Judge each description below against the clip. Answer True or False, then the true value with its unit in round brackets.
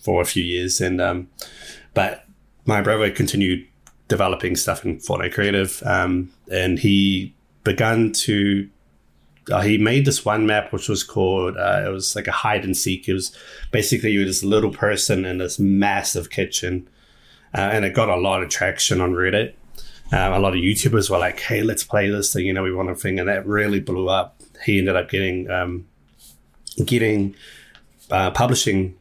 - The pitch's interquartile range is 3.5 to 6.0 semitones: False (2.5 semitones)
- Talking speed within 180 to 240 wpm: True (185 wpm)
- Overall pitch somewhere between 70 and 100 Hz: True (95 Hz)